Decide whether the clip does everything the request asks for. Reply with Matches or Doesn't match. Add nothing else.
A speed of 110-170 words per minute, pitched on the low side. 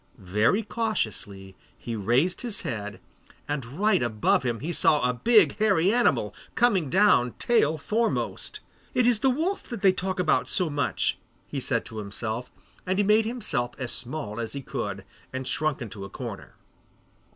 Doesn't match